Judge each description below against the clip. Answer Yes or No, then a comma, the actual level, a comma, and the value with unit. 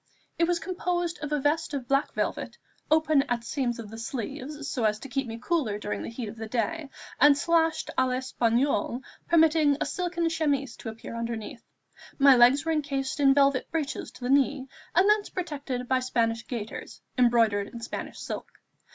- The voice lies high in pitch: Yes, very high, 275 Hz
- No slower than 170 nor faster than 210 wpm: Yes, average, 185 wpm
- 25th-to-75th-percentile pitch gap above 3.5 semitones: Yes, average, 4.7 semitones